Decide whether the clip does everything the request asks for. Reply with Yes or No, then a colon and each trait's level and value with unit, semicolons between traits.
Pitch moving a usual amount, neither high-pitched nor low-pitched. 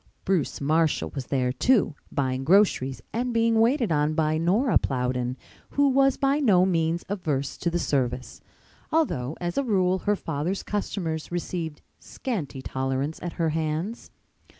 No: wide, 6.6 semitones; medium, 165 Hz